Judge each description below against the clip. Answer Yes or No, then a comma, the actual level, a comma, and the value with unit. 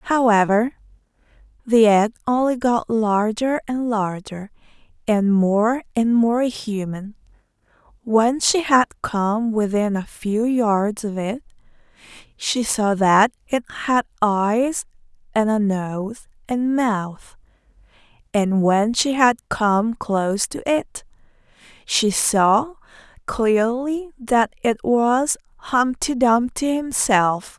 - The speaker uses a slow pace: Yes, slow, 110 wpm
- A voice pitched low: No, high, 225 Hz